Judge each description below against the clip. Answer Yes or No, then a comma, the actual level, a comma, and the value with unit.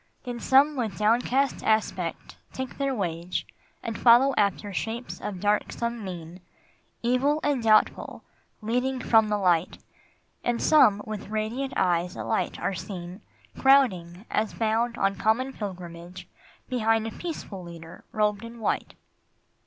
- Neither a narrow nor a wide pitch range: Yes, average, 4.6 semitones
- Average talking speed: No, slow, 130 wpm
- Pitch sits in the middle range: No, high, 220 Hz